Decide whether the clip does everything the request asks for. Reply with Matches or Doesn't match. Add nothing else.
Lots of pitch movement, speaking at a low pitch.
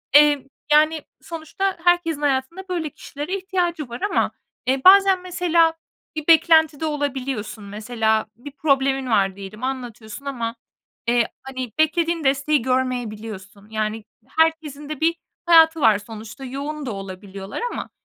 Doesn't match